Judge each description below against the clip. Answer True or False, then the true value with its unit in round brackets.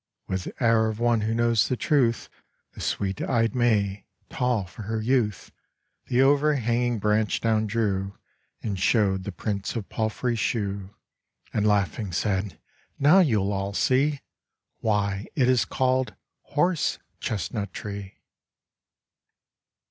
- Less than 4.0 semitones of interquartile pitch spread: True (3.4 semitones)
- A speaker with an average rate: False (125 wpm)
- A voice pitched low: True (110 Hz)